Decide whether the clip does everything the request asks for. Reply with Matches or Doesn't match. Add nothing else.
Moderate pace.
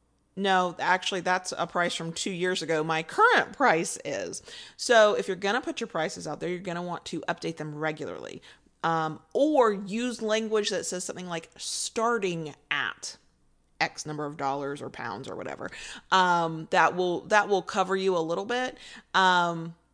Matches